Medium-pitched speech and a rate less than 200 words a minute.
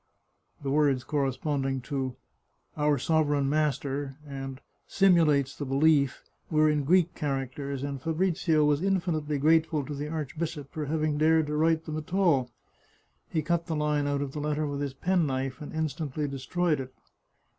Yes: medium, 150 Hz; average, 160 wpm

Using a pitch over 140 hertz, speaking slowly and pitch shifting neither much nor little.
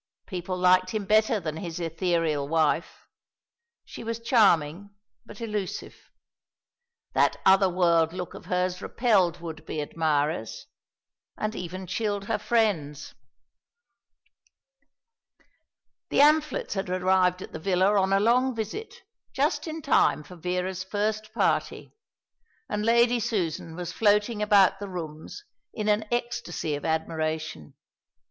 Yes: medium, 185 Hz; slow, 125 wpm; average, 4.4 semitones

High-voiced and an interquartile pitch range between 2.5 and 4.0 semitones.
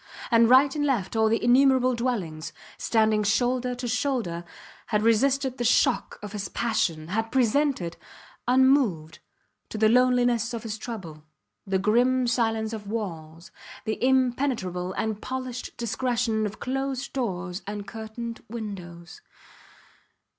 Yes: high, 230 Hz; average, 3.7 semitones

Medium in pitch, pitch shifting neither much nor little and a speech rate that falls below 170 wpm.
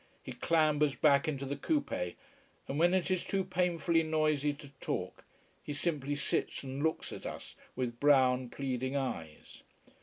Yes: medium, 145 Hz; average, 3.4 semitones; average, 155 wpm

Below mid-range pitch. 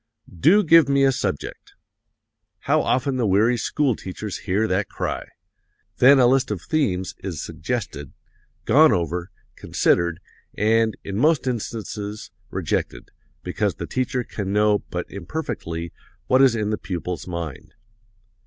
Yes: low, 105 Hz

